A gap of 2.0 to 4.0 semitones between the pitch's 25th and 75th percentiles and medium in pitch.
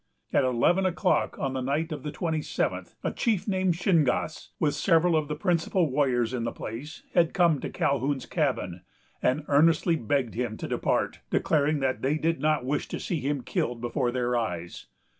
No: average, 4.4 semitones; medium, 145 Hz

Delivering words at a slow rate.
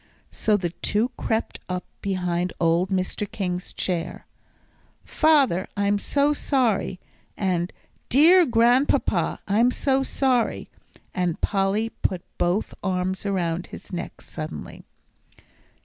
Yes: slow, 110 wpm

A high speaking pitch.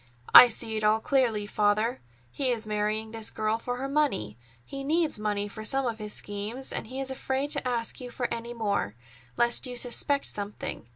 Yes: high, 230 Hz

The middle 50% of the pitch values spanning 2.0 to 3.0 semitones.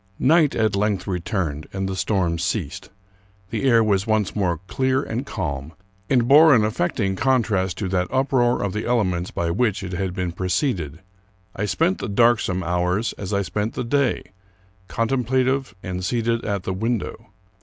No: average, 4.7 semitones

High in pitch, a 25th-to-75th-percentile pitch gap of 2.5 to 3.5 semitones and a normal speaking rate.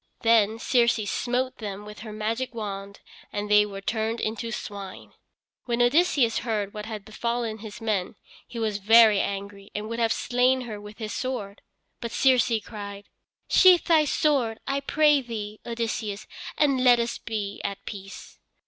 Yes: high, 225 Hz; average, 2.8 semitones; average, 160 wpm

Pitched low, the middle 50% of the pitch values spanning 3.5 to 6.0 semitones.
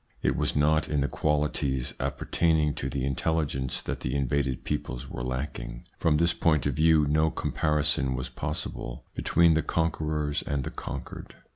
No: very low, 75 Hz; average, 2.8 semitones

